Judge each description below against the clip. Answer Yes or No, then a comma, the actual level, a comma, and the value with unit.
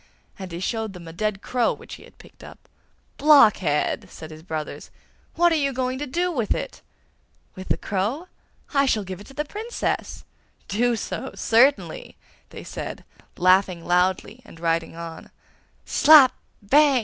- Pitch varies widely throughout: Yes, wide, 7.4 semitones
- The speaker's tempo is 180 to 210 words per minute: No, average, 160 wpm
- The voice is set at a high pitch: Yes, high, 220 Hz